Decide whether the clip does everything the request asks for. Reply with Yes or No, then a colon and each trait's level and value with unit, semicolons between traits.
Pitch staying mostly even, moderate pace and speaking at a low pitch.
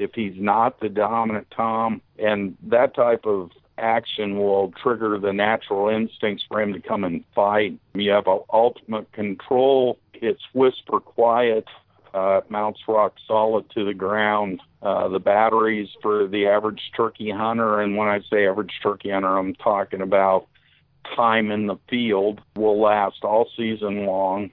Yes: narrow, 1.8 semitones; average, 155 wpm; low, 105 Hz